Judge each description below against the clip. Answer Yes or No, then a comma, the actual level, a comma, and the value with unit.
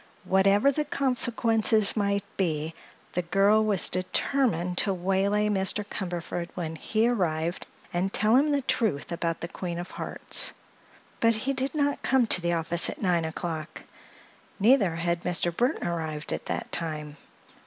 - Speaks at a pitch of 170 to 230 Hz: Yes, high, 190 Hz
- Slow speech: No, average, 155 wpm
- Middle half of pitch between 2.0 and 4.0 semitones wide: No, average, 4.4 semitones